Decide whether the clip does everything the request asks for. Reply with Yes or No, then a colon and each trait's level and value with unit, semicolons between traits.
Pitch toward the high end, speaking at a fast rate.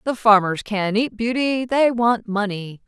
No: high, 220 Hz; average, 165 wpm